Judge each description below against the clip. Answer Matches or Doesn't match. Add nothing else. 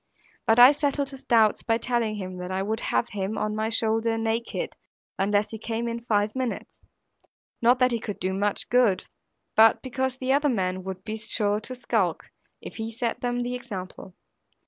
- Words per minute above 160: Matches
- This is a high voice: Matches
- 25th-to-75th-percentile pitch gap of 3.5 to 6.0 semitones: Doesn't match